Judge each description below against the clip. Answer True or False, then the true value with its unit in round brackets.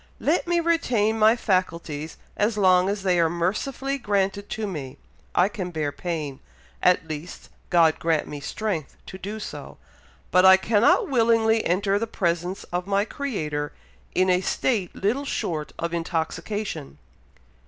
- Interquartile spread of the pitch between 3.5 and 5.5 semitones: True (4.6 semitones)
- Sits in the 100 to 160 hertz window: False (190 Hz)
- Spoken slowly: False (150 wpm)